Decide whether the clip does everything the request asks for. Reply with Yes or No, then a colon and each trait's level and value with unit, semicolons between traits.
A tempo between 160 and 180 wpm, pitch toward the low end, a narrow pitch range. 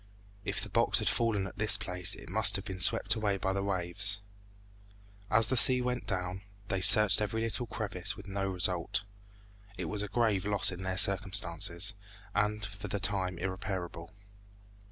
Yes: average, 175 wpm; low, 100 Hz; narrow, 2.3 semitones